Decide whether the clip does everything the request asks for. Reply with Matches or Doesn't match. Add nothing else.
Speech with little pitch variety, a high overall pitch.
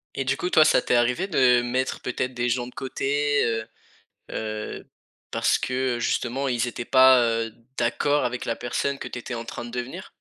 Doesn't match